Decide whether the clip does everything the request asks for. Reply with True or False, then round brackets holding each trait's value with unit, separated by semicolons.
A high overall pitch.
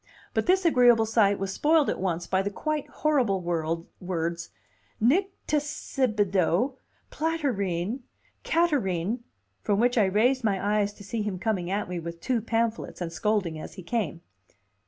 True (210 Hz)